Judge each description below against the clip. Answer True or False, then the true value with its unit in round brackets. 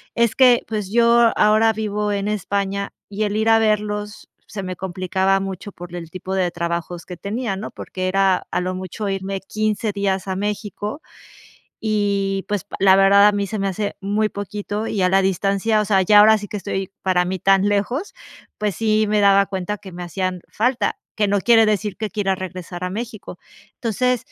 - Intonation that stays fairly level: True (1.9 semitones)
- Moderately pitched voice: False (200 Hz)